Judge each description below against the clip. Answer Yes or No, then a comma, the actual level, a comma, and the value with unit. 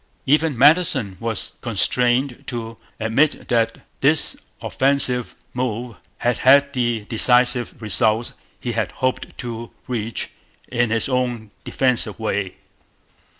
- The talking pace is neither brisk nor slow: No, slow, 110 wpm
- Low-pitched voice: Yes, low, 120 Hz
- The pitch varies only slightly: Yes, narrow, 2.2 semitones